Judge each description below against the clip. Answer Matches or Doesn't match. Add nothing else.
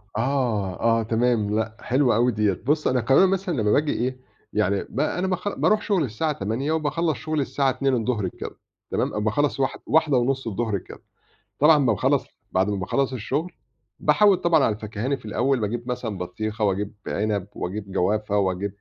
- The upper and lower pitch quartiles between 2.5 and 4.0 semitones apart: Doesn't match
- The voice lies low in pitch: Matches